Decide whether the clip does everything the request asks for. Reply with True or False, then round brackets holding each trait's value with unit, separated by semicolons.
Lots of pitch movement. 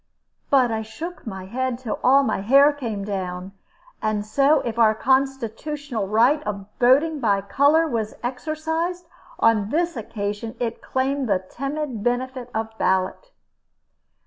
False (4.8 semitones)